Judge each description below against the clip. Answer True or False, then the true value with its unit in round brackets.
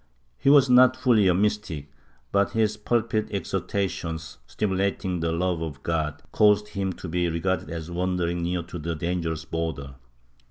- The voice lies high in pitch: False (90 Hz)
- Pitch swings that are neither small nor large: True (3.9 semitones)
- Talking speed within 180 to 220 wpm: False (155 wpm)